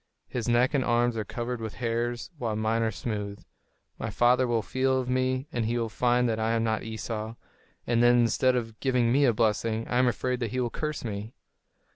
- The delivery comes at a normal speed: No, fast, 215 wpm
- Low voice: Yes, low, 120 Hz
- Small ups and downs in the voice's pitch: Yes, narrow, 1.8 semitones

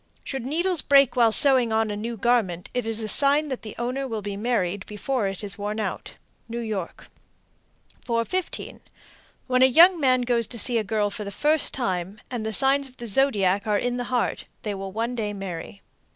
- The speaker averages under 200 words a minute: No, fast, 205 wpm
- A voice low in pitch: No, high, 230 Hz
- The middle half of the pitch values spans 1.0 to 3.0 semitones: No, average, 3.8 semitones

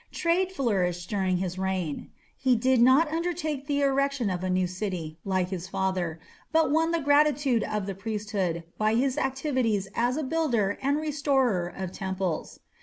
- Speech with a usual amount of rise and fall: No, wide, 7.1 semitones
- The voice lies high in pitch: Yes, high, 225 Hz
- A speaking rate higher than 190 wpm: No, average, 165 wpm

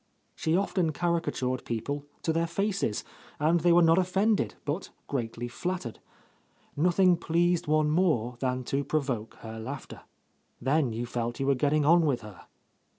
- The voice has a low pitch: No, medium, 150 Hz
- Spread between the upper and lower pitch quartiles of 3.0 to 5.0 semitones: No, wide, 5.5 semitones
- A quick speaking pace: No, average, 155 wpm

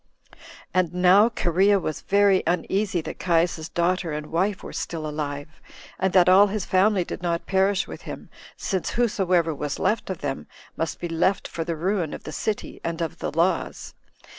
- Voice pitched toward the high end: No, medium, 180 Hz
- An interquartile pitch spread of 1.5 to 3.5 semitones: Yes, average, 2.9 semitones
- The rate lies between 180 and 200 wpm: Yes, average, 185 wpm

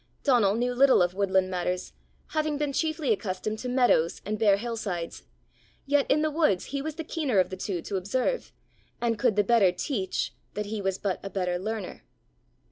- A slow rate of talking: No, average, 195 wpm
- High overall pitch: Yes, high, 215 Hz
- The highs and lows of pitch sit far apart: Yes, wide, 5.9 semitones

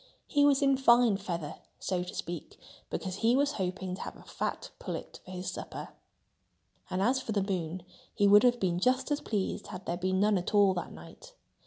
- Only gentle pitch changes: No, average, 5.1 semitones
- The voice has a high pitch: Yes, high, 195 Hz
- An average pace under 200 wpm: No, fast, 205 wpm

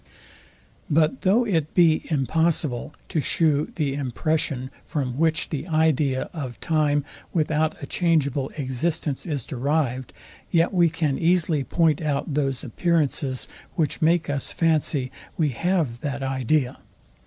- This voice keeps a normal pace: No, slow, 130 wpm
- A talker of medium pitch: Yes, medium, 150 Hz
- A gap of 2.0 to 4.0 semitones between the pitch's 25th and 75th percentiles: Yes, average, 3.2 semitones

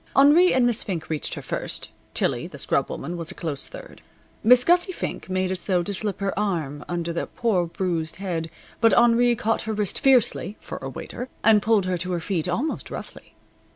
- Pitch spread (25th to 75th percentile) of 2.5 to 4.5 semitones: No, wide, 5.4 semitones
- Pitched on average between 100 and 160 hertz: No, high, 195 Hz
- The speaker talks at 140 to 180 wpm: No, fast, 205 wpm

